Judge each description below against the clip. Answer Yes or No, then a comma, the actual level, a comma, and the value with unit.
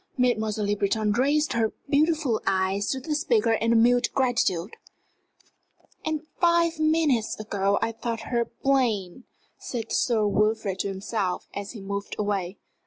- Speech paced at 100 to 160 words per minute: Yes, average, 145 wpm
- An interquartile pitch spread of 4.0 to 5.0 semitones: Yes, average, 4.7 semitones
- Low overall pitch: No, high, 225 Hz